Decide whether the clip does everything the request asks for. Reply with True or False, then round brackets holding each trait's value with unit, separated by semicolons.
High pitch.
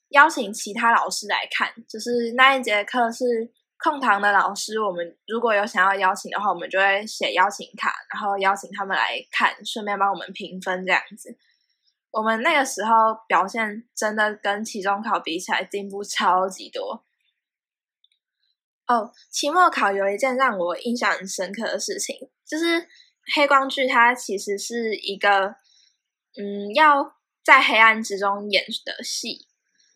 True (220 Hz)